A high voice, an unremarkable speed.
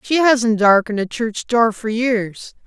Yes: high, 225 Hz; average, 180 wpm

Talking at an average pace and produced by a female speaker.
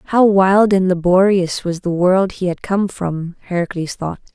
Yes: average, 180 wpm; female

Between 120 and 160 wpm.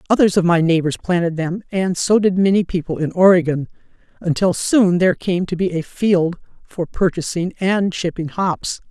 No: average, 175 wpm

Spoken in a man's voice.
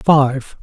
Yes: male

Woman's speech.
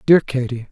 No: male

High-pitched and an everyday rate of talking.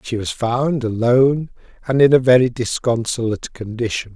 No: low, 120 Hz; average, 145 wpm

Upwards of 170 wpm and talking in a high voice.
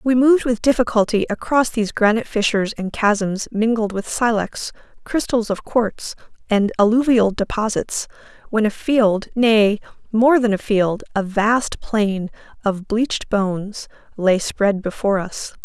No: average, 140 wpm; high, 215 Hz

